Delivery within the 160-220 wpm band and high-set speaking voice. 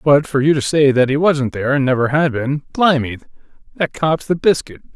No: fast, 205 wpm; medium, 140 Hz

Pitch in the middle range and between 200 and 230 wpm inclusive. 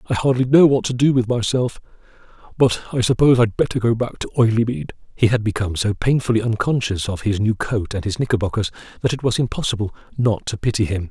No: low, 115 Hz; fast, 205 wpm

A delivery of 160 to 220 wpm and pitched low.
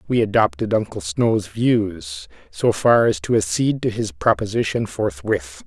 No: average, 150 wpm; low, 110 Hz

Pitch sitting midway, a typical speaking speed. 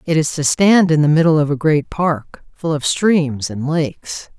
No: medium, 155 Hz; fast, 220 wpm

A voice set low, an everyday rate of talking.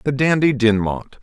Yes: low, 125 Hz; average, 145 wpm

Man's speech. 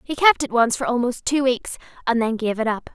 No: female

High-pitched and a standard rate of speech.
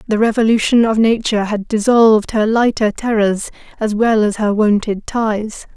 Yes: high, 215 Hz; average, 155 wpm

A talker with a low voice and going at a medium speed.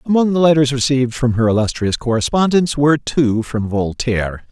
Yes: low, 130 Hz; average, 160 wpm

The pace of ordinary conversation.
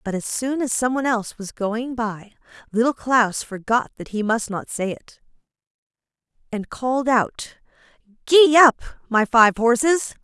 Yes: average, 150 wpm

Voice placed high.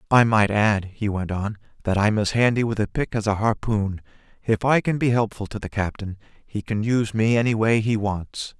No: low, 110 Hz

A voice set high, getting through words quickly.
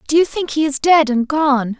Yes: very high, 290 Hz; fast, 265 wpm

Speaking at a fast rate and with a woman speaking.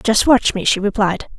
Yes: fast, 215 wpm; female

